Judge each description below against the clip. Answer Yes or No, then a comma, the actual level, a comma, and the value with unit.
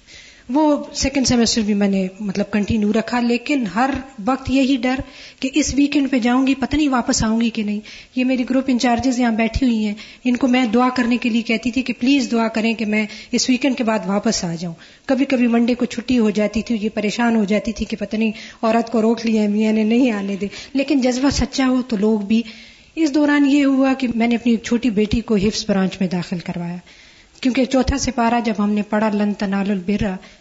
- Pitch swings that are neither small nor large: Yes, average, 3.2 semitones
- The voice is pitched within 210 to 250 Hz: Yes, high, 235 Hz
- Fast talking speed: Yes, fast, 225 wpm